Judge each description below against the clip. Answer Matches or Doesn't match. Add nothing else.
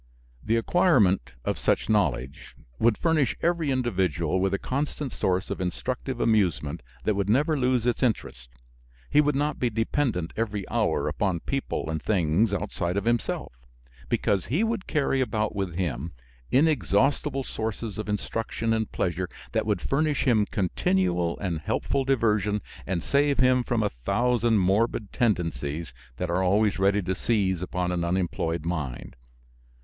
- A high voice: Doesn't match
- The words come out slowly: Doesn't match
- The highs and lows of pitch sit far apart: Matches